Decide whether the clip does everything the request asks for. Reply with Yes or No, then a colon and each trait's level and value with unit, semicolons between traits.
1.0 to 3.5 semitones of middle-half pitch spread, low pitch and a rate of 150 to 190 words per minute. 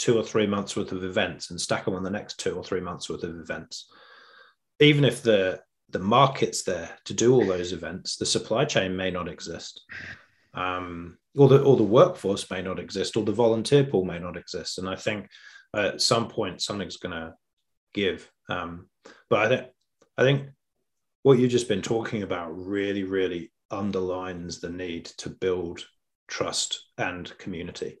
No: average, 4.3 semitones; very low, 95 Hz; average, 180 wpm